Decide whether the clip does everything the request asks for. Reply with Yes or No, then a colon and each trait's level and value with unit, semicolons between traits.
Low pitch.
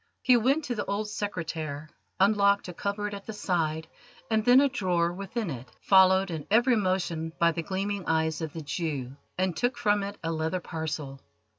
No: medium, 185 Hz